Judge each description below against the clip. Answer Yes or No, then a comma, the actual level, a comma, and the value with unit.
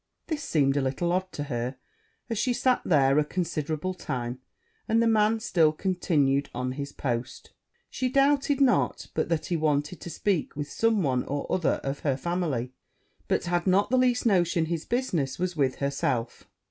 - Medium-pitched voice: Yes, medium, 165 Hz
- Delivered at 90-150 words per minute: No, average, 180 wpm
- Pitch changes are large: Yes, wide, 6.6 semitones